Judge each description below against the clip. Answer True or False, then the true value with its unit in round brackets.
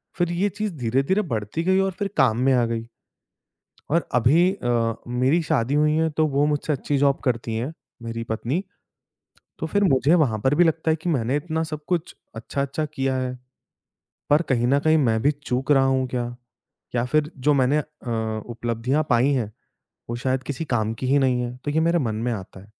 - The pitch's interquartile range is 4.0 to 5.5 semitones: True (4.5 semitones)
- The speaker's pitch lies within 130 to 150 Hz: True (135 Hz)